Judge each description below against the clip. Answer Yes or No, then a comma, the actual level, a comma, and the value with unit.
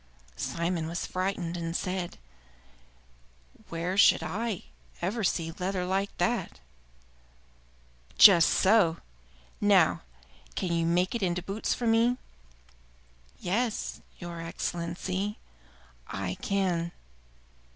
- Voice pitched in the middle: Yes, medium, 180 Hz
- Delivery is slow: Yes, slow, 100 wpm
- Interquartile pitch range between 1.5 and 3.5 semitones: Yes, average, 2.8 semitones